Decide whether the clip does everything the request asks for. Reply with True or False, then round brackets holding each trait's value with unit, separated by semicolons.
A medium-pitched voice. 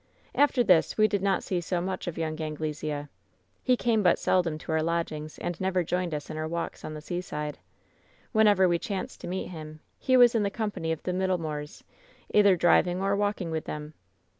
True (175 Hz)